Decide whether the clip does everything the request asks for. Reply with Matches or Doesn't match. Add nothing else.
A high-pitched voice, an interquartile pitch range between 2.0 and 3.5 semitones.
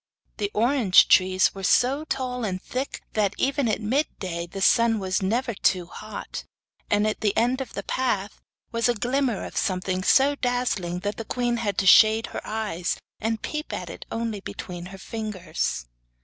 Doesn't match